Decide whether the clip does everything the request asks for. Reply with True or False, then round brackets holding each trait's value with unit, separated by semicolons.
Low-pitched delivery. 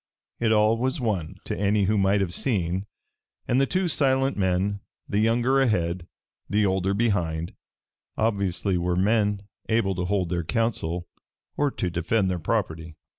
True (100 Hz)